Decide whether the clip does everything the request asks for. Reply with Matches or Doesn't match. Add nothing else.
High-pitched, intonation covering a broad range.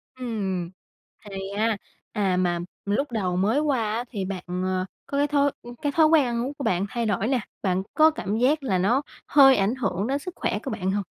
Matches